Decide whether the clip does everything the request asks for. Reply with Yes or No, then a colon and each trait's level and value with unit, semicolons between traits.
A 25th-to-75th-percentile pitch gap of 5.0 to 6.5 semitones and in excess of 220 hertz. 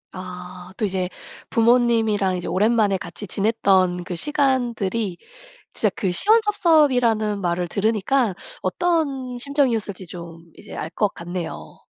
No: average, 5.3 semitones; high, 210 Hz